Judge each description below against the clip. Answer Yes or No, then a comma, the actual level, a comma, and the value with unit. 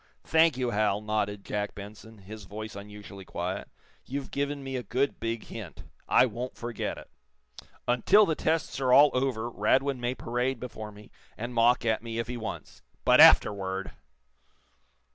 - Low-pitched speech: Yes, low, 115 Hz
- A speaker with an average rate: Yes, average, 160 wpm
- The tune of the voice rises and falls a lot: No, average, 3.6 semitones